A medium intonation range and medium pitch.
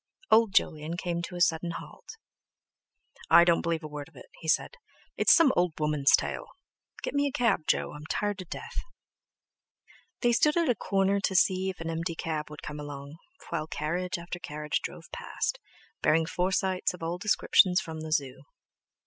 Yes: average, 3.8 semitones; medium, 170 Hz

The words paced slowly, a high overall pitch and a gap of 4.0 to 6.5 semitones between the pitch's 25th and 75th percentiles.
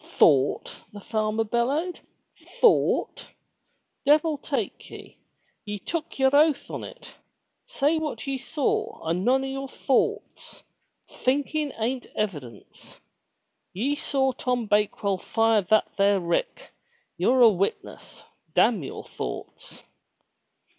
Yes: slow, 115 wpm; very high, 250 Hz; wide, 5.6 semitones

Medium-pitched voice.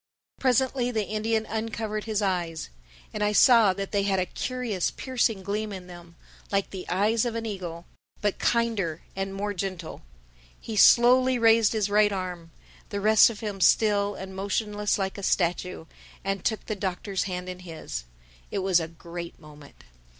No: high, 200 Hz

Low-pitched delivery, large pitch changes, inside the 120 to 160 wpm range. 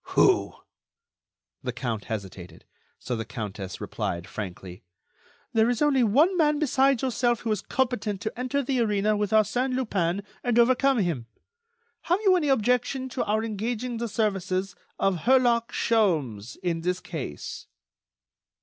No: high, 220 Hz; wide, 7.2 semitones; average, 140 wpm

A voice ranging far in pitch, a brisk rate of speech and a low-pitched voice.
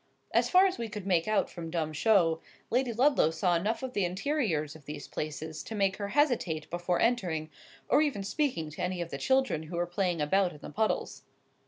No: wide, 6.1 semitones; fast, 210 wpm; medium, 185 Hz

